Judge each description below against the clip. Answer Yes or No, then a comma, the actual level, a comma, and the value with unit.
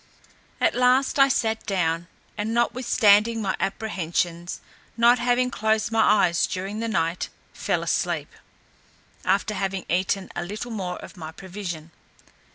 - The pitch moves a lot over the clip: No, average, 4.3 semitones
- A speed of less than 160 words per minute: Yes, slow, 135 wpm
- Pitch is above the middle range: Yes, high, 210 Hz